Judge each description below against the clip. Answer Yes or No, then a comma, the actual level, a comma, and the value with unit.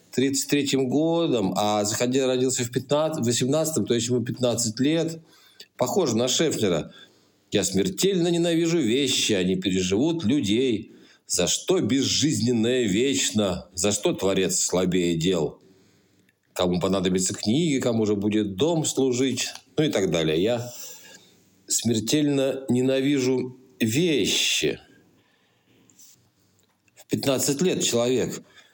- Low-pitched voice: Yes, low, 125 Hz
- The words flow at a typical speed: No, slow, 105 wpm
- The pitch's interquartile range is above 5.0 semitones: Yes, wide, 5.5 semitones